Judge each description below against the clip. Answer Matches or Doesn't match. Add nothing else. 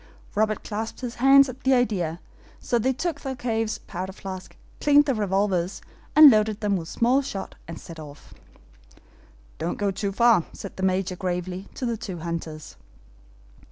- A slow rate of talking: Doesn't match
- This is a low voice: Doesn't match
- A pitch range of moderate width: Matches